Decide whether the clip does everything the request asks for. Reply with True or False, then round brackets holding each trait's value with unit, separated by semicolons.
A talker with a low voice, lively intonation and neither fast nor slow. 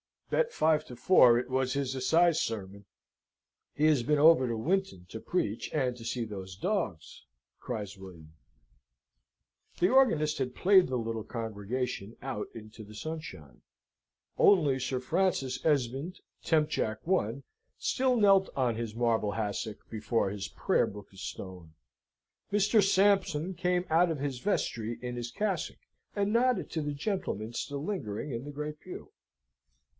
True (130 Hz; 7.7 semitones; 150 wpm)